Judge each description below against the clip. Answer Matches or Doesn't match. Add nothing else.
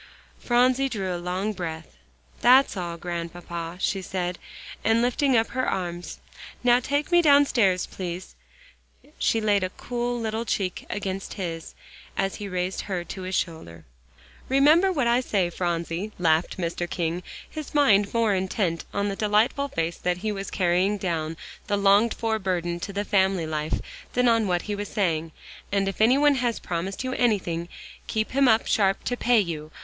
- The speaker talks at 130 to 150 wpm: Doesn't match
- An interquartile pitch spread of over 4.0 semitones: Matches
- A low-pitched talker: Doesn't match